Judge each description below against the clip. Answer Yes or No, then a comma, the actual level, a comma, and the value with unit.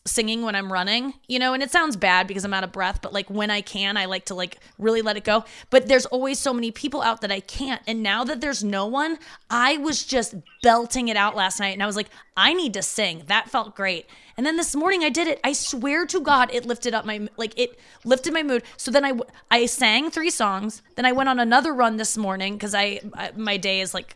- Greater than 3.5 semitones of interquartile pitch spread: Yes, average, 4.6 semitones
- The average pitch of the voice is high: Yes, high, 230 Hz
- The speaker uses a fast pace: Yes, fast, 260 wpm